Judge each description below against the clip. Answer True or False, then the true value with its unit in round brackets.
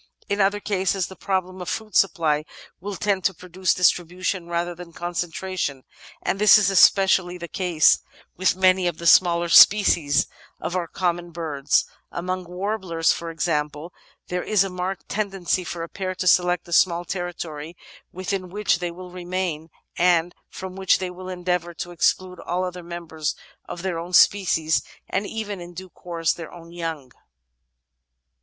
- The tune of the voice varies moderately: False (1.7 semitones)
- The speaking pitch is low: False (180 Hz)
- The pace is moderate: True (165 wpm)